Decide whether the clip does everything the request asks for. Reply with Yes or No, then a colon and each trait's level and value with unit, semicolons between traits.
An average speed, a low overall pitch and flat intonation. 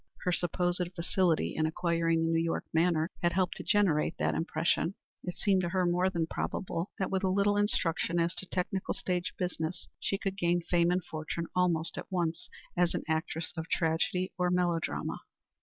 No: average, 185 wpm; medium, 175 Hz; narrow, 1.8 semitones